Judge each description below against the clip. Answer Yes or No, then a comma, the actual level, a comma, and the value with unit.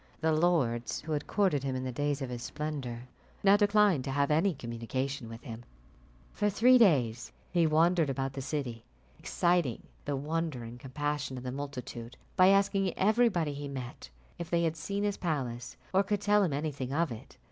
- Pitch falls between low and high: Yes, medium, 145 Hz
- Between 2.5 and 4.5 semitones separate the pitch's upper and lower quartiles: No, wide, 5.5 semitones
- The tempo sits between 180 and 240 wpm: Yes, average, 185 wpm